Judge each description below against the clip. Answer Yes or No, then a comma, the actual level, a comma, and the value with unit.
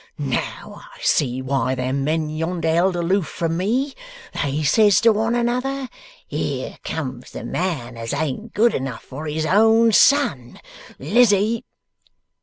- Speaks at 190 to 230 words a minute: No, average, 140 wpm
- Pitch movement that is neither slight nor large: No, wide, 8.2 semitones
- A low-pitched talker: No, medium, 170 Hz